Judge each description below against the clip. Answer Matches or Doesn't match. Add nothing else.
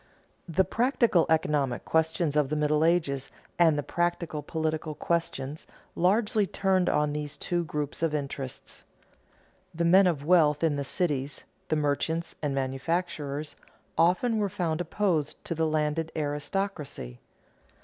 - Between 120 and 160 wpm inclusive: Matches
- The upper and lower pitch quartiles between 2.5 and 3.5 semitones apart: Matches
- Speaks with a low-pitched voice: Doesn't match